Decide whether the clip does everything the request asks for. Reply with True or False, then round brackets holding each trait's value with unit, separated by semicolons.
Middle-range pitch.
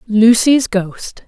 False (220 Hz)